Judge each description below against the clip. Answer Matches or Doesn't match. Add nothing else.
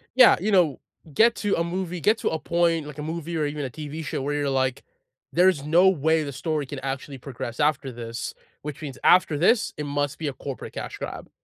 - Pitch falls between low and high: Matches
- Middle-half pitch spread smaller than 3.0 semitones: Doesn't match